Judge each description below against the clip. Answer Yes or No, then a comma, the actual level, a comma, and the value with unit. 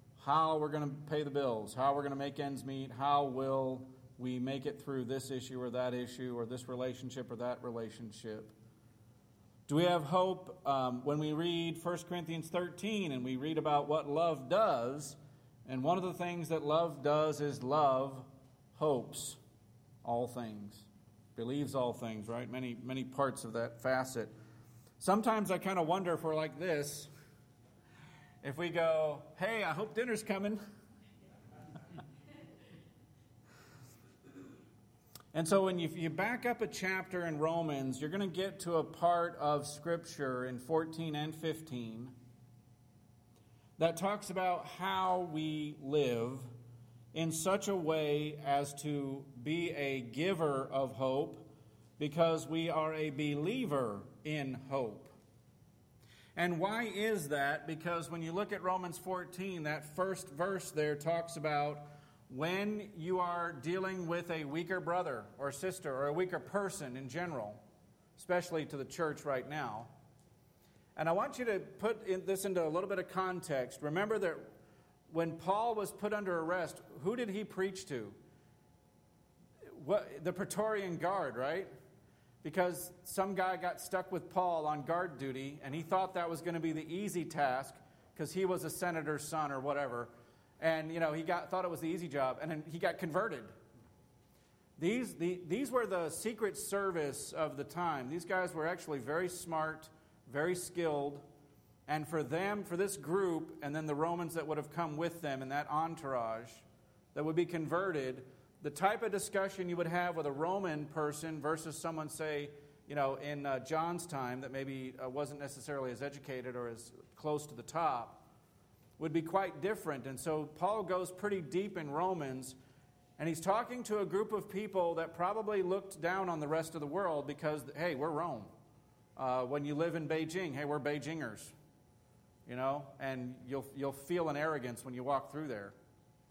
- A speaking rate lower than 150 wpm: No, average, 170 wpm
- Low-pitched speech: No, medium, 155 Hz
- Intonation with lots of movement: No, average, 4.7 semitones